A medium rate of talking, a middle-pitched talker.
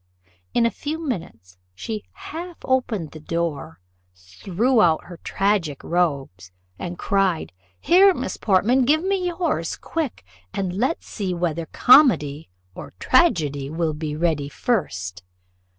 No: slow, 130 wpm; medium, 180 Hz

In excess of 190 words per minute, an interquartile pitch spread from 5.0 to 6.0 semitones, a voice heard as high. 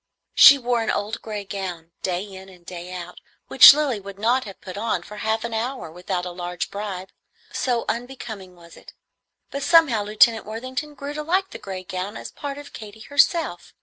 Yes: average, 200 wpm; wide, 5.6 semitones; high, 210 Hz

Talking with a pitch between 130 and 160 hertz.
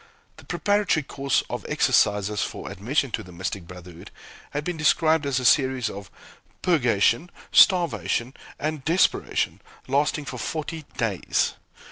Yes: low, 135 Hz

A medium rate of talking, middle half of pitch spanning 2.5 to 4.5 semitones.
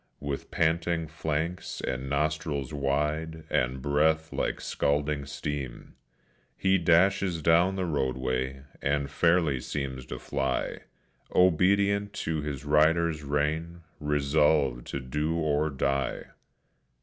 No: slow, 110 wpm; average, 2.9 semitones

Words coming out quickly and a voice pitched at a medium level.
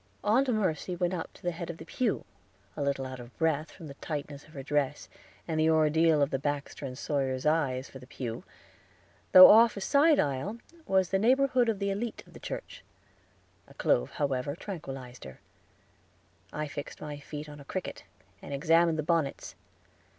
No: average, 190 wpm; medium, 155 Hz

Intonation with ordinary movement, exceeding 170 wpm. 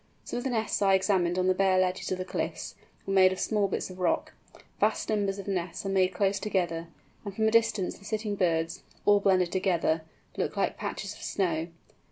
No: narrow, 1.9 semitones; fast, 205 wpm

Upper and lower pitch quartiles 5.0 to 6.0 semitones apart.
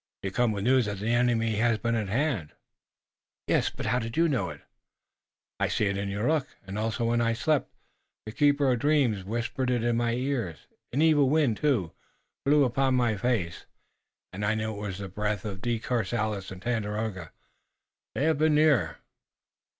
No: average, 4.1 semitones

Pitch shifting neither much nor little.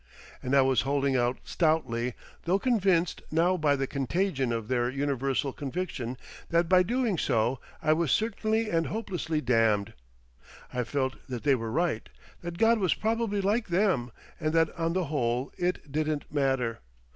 No: wide, 5.8 semitones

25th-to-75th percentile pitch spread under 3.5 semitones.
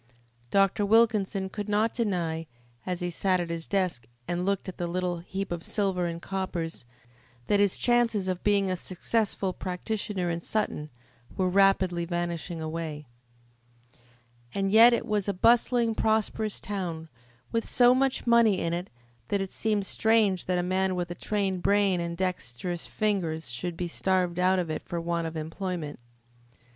Yes: average, 3.1 semitones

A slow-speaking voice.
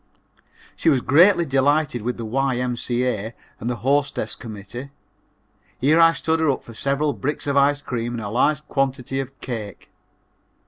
No: average, 155 wpm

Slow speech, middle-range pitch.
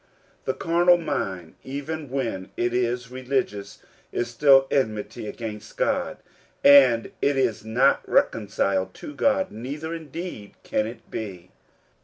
No: slow, 125 wpm; low, 125 Hz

